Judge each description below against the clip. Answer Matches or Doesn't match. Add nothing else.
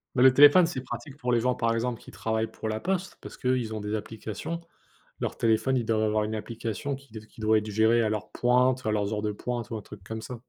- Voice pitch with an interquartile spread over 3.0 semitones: Doesn't match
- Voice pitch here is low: Matches